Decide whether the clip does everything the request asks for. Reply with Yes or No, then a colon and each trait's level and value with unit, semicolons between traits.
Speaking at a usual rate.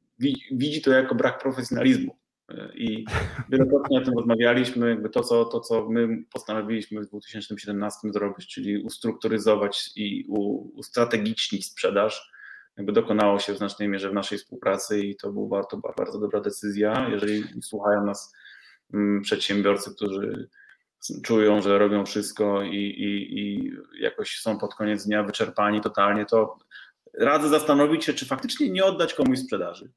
Yes: average, 140 wpm